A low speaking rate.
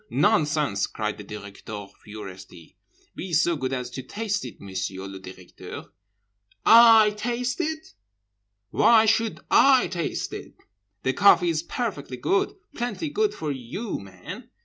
Yes: slow, 125 wpm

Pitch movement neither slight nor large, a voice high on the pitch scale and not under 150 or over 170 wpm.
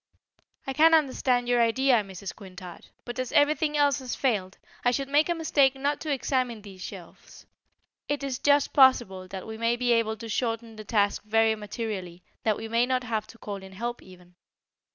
No: average, 4.4 semitones; high, 235 Hz; average, 195 wpm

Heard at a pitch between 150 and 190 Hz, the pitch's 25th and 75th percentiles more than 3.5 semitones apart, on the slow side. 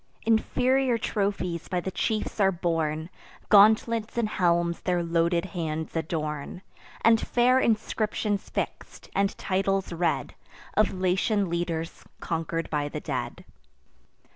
Yes: medium, 185 Hz; average, 4.2 semitones; slow, 115 wpm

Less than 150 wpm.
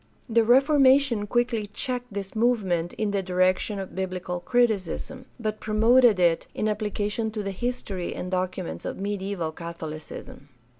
Yes: average, 140 wpm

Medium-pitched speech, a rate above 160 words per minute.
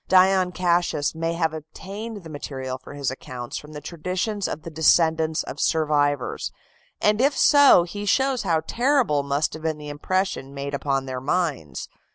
Yes: medium, 160 Hz; average, 170 wpm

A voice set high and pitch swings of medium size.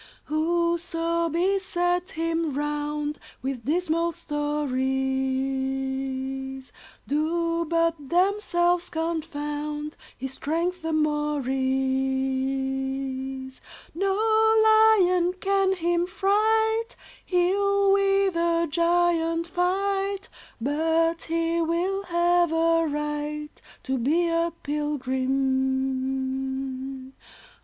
Yes: very high, 325 Hz; average, 4.7 semitones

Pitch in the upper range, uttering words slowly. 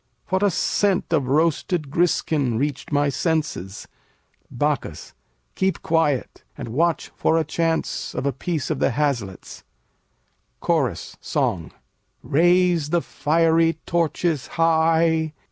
No: medium, 160 Hz; slow, 115 wpm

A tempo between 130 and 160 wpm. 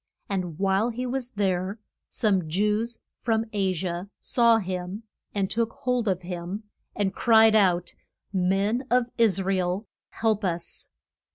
Yes: average, 150 wpm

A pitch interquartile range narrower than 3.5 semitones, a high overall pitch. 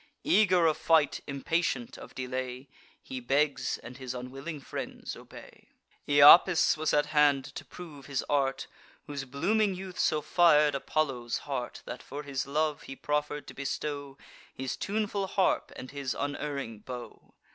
No: average, 2.8 semitones; medium, 145 Hz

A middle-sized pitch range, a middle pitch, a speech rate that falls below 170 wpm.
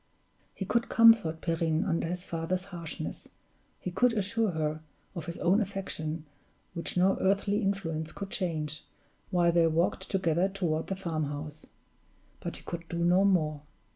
Yes: average, 3.2 semitones; medium, 175 Hz; average, 150 wpm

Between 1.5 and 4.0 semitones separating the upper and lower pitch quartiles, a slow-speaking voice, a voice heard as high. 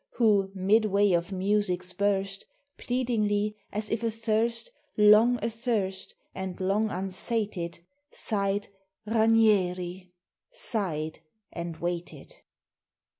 Yes: average, 3.1 semitones; slow, 85 wpm; high, 205 Hz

